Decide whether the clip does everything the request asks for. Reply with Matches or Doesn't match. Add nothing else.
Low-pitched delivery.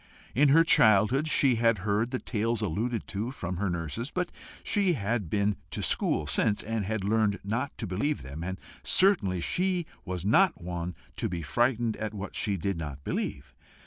Matches